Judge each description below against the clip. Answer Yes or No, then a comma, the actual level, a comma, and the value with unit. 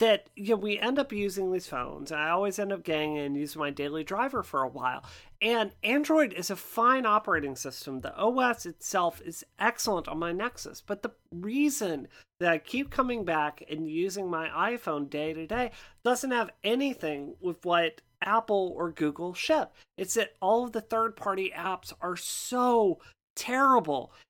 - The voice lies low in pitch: No, high, 195 Hz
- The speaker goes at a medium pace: Yes, average, 180 wpm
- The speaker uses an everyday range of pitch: No, wide, 6.5 semitones